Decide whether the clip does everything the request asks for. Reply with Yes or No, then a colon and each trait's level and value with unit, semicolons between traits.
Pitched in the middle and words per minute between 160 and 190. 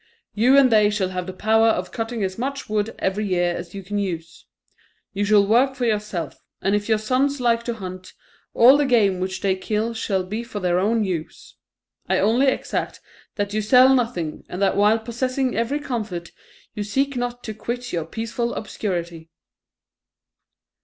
No: high, 215 Hz; average, 180 wpm